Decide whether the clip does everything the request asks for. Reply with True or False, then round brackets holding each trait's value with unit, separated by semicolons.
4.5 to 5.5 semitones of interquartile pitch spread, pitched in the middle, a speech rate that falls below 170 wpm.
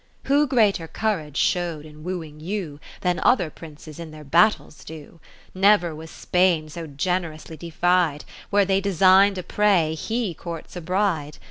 False (3.8 semitones; 175 Hz; 140 wpm)